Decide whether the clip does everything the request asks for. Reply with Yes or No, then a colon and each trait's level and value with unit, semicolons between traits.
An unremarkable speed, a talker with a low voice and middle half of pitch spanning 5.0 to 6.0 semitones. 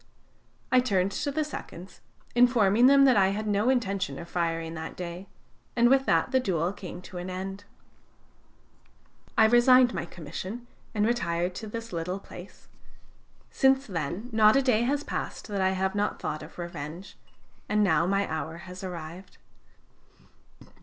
No: average, 160 wpm; high, 195 Hz; average, 5.3 semitones